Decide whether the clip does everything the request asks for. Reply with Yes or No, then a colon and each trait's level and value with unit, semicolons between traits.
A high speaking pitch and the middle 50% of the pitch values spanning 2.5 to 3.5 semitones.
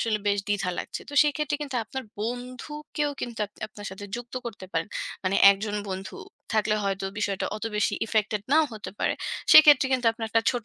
No: high, 220 Hz; average, 4.2 semitones